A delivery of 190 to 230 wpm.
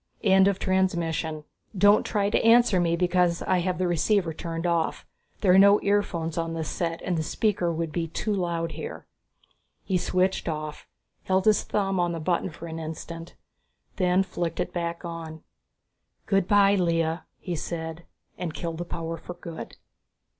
No: average, 170 wpm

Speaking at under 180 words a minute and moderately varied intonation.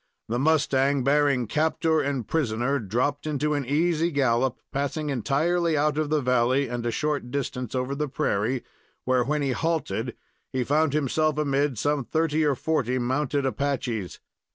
Yes: average, 155 wpm; average, 3.1 semitones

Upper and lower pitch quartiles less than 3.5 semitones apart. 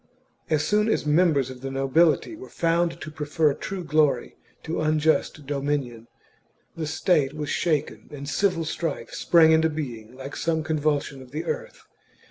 Yes: average, 2.8 semitones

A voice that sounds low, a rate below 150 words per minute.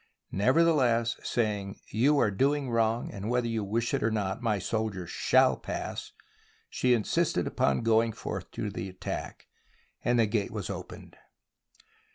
No: low, 115 Hz; average, 165 wpm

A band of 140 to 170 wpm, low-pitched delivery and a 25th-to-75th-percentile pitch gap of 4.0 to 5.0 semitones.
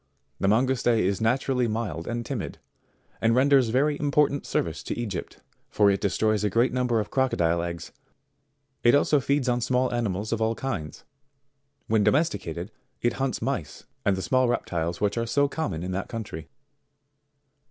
Yes: average, 165 wpm; low, 115 Hz; average, 4.7 semitones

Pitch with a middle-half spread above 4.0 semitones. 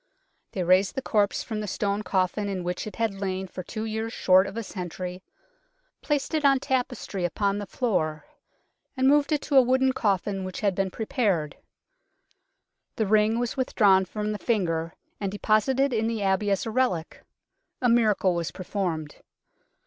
No: average, 3.7 semitones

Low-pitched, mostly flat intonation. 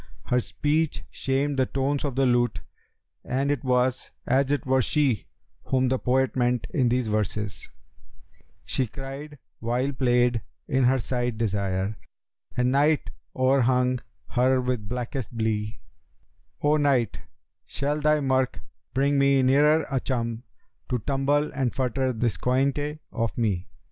Yes: low, 130 Hz; narrow, 2.2 semitones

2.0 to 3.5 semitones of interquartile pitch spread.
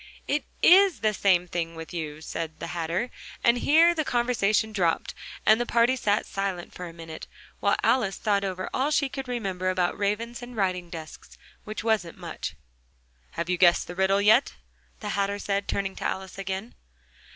No: average, 4.8 semitones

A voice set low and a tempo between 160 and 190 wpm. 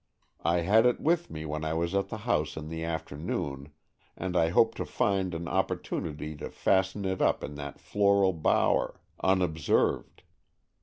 Yes: very low, 85 Hz; average, 165 wpm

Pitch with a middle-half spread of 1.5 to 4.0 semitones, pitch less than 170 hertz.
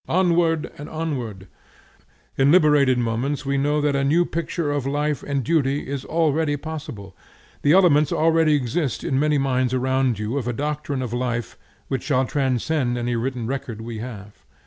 Yes: average, 3.4 semitones; medium, 140 Hz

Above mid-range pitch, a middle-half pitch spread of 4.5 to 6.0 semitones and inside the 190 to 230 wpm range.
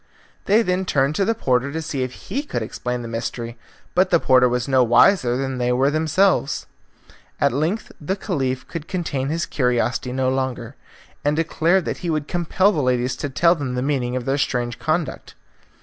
No: low, 135 Hz; average, 5.0 semitones; average, 195 wpm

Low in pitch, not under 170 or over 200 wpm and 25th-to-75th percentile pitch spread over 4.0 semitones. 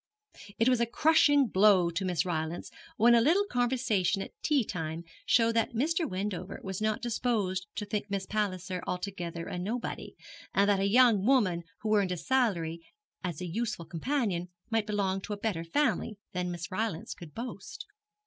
No: high, 200 Hz; average, 175 wpm; average, 4.6 semitones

